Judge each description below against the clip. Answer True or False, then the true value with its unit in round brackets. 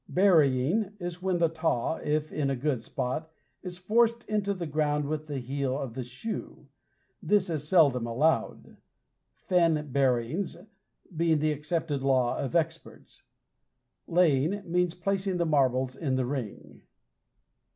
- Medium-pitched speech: True (155 Hz)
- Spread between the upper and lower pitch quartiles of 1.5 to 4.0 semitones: False (4.7 semitones)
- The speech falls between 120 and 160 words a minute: True (140 wpm)